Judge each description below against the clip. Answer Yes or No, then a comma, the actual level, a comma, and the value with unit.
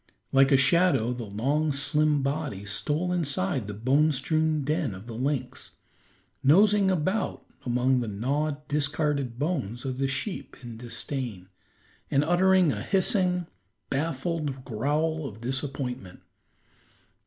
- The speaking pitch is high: No, medium, 140 Hz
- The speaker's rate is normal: No, slow, 125 wpm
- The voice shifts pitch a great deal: No, average, 4.1 semitones